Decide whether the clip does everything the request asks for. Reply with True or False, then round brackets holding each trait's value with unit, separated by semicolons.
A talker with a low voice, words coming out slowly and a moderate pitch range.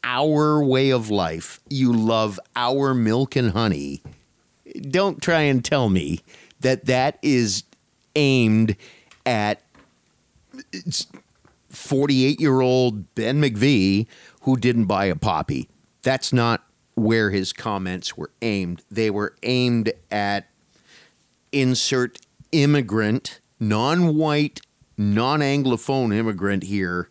True (120 Hz; 110 wpm; 4.4 semitones)